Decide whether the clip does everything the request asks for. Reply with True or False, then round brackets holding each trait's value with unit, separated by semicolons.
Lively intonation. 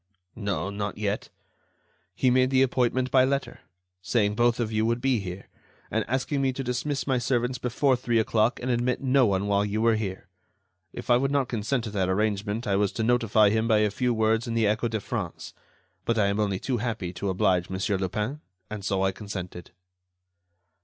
False (3.6 semitones)